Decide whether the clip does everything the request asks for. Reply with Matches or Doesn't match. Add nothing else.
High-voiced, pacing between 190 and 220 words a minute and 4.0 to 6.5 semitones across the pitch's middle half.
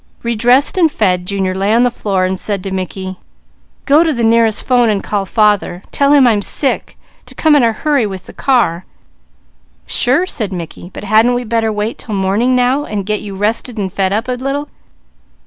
Matches